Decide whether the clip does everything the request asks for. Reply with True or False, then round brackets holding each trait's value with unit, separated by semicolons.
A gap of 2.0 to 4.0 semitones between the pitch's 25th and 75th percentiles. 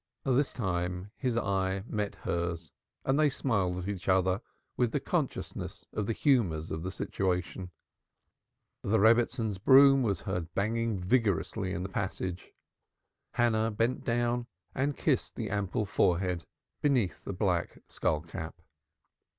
False (4.6 semitones)